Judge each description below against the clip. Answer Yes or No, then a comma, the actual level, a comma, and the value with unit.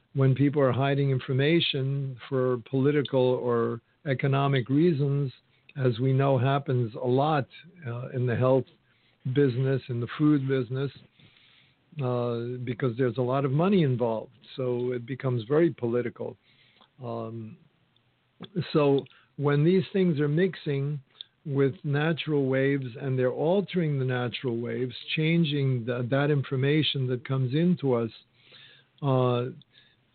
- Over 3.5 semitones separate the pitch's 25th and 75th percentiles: No, narrow, 2.5 semitones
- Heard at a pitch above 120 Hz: Yes, low, 135 Hz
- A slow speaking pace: Yes, slow, 125 wpm